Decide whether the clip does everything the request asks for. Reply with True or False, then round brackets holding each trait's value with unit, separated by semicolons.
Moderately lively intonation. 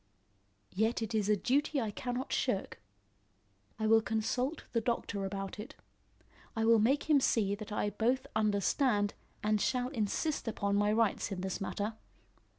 True (3.2 semitones)